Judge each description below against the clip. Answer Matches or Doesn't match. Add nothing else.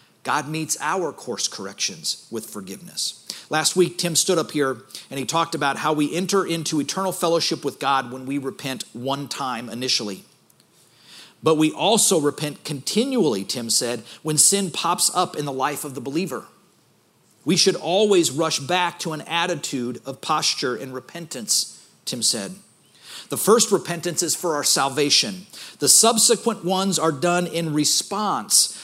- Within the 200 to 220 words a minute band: Doesn't match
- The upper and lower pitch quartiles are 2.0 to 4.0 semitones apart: Doesn't match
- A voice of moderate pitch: Matches